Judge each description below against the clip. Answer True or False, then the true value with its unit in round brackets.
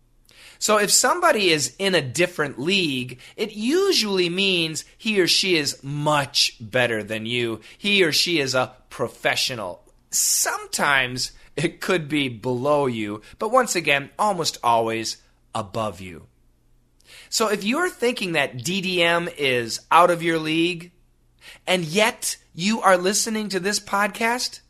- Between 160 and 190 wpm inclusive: False (140 wpm)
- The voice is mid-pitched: True (165 Hz)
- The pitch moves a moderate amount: False (8.2 semitones)